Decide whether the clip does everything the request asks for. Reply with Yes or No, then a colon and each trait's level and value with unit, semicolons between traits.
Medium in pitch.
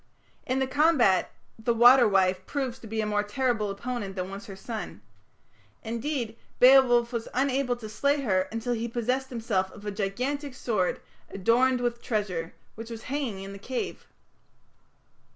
No: high, 230 Hz